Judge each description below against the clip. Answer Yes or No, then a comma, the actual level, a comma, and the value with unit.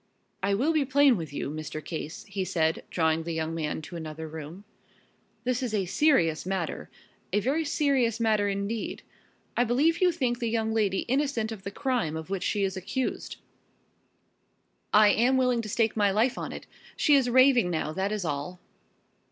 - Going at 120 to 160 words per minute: No, average, 185 wpm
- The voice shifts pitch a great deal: Yes, wide, 6.7 semitones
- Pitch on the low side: No, high, 210 Hz